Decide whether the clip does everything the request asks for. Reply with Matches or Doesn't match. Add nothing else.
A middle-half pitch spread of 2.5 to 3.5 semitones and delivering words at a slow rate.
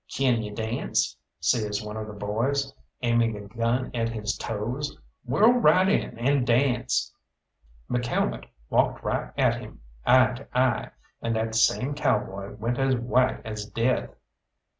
Doesn't match